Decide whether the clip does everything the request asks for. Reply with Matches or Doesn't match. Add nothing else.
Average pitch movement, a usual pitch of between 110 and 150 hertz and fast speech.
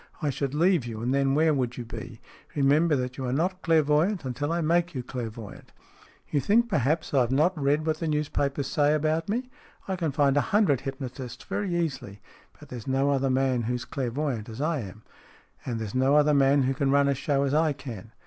Matches